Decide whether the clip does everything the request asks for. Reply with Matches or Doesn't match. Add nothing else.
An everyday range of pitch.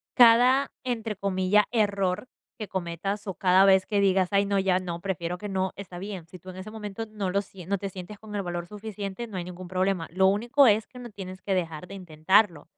Doesn't match